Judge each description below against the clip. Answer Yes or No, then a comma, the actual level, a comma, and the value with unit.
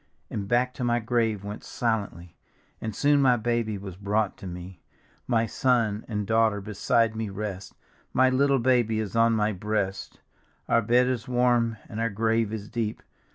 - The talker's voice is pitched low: Yes, low, 110 Hz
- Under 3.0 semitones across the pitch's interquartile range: Yes, narrow, 2.6 semitones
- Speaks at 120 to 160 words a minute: No, average, 170 wpm